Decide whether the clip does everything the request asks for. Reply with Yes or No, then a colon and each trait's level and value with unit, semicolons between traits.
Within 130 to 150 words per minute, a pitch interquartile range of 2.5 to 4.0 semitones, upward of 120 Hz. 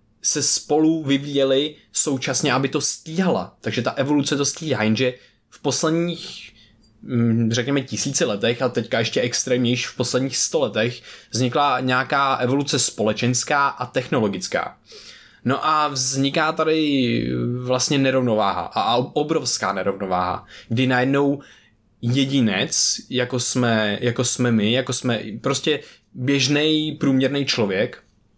No: slow, 115 wpm; average, 2.9 semitones; low, 130 Hz